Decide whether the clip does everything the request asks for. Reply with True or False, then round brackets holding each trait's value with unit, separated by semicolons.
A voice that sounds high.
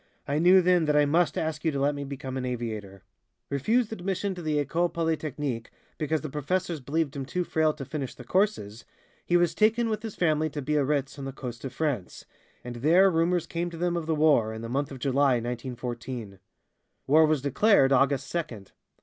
False (150 Hz)